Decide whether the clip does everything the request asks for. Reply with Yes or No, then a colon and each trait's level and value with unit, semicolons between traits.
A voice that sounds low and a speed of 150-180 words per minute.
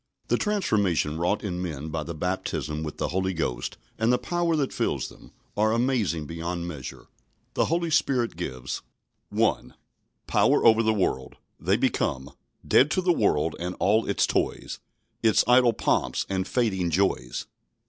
Yes: very low, 95 Hz; average, 160 wpm